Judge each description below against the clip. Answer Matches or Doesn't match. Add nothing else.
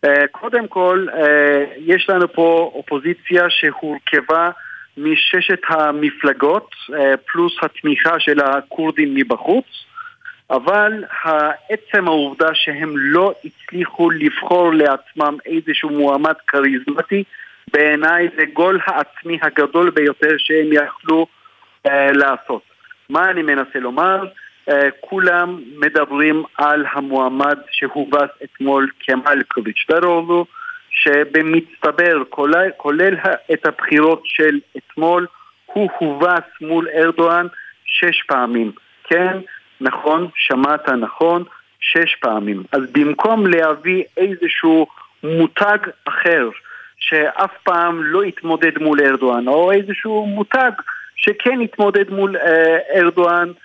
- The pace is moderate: Doesn't match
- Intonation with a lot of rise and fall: Doesn't match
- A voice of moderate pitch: Matches